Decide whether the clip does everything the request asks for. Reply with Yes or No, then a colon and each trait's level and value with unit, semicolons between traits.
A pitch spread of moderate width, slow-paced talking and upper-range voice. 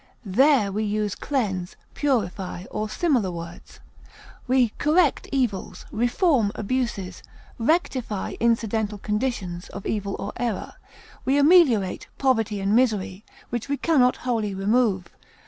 Yes: average, 4.6 semitones; slow, 120 wpm; high, 220 Hz